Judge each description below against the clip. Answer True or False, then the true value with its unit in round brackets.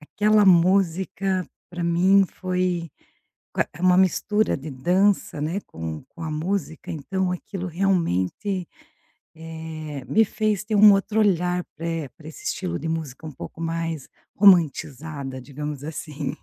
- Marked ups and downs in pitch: False (3.8 semitones)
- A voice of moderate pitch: True (170 Hz)